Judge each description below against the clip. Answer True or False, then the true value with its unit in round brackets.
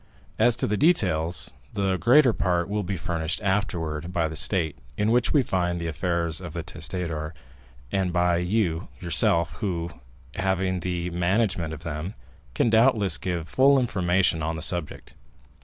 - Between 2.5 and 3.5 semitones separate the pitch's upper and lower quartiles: True (3.1 semitones)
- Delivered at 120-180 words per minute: True (155 wpm)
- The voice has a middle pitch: False (90 Hz)